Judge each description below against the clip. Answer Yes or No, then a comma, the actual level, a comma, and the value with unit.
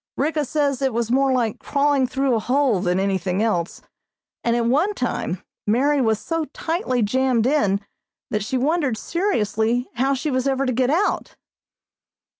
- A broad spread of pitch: No, average, 4.2 semitones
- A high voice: Yes, very high, 255 Hz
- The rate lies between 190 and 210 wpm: No, average, 165 wpm